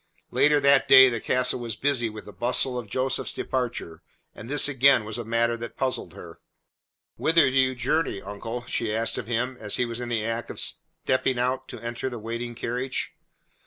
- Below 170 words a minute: No, average, 200 wpm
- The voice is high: No, low, 120 Hz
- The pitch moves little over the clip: Yes, narrow, 2.3 semitones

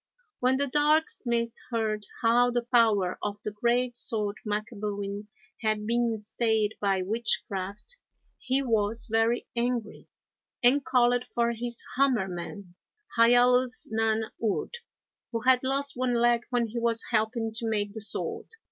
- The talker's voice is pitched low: No, high, 230 Hz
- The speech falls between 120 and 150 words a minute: Yes, average, 140 wpm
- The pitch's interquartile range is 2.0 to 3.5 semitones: Yes, narrow, 2.5 semitones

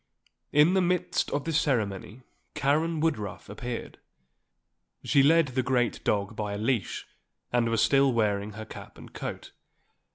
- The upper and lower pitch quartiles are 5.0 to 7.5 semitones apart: Yes, wide, 5.6 semitones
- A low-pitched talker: Yes, low, 125 Hz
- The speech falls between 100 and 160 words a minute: Yes, average, 150 wpm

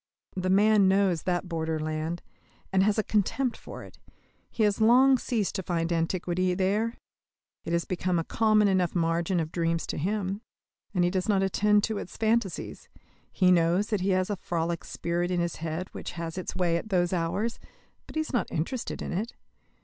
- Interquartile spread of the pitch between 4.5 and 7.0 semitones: No, average, 3.5 semitones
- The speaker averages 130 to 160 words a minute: No, average, 190 wpm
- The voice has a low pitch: No, medium, 185 Hz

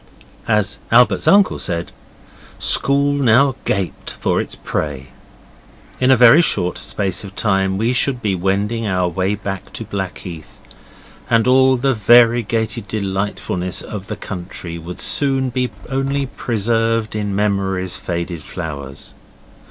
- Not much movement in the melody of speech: No, average, 4.7 semitones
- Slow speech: Yes, slow, 130 wpm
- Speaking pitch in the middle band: No, low, 105 Hz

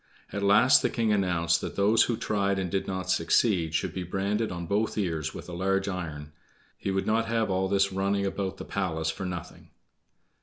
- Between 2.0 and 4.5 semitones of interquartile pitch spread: Yes, narrow, 2.4 semitones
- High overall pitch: No, very low, 95 Hz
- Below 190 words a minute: No, average, 200 wpm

